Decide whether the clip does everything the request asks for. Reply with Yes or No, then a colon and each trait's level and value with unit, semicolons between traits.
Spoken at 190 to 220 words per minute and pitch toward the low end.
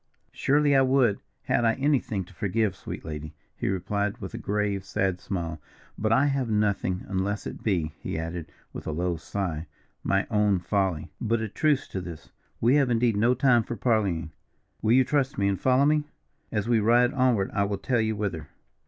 Yes: average, 195 wpm; low, 105 Hz